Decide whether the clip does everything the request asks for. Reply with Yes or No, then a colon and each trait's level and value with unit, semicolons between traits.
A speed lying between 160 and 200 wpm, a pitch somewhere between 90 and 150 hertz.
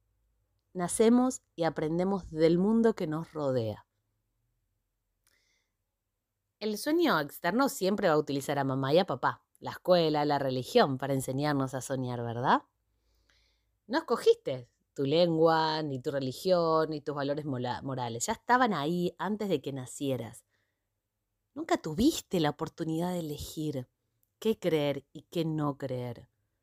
No: average, 135 wpm; medium, 140 Hz